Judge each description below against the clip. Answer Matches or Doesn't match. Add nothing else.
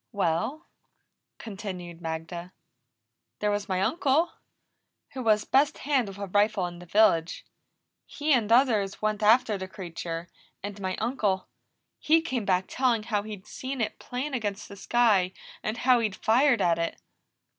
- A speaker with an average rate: Matches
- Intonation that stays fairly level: Doesn't match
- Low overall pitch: Doesn't match